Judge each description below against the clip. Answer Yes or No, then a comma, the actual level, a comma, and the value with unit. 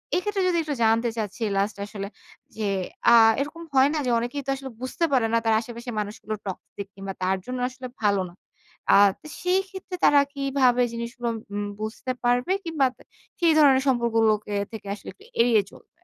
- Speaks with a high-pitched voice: Yes, high, 245 Hz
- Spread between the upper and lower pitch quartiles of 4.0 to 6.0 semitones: Yes, average, 4.5 semitones